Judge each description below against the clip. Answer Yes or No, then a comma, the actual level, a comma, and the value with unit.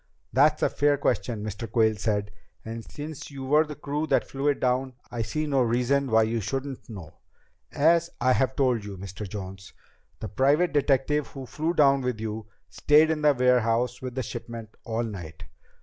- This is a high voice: No, low, 125 Hz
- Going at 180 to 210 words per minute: Yes, average, 185 wpm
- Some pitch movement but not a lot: Yes, average, 4.3 semitones